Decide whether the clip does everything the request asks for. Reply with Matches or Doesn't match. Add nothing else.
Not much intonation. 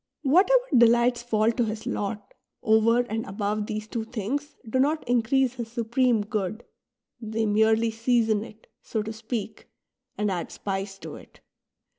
Matches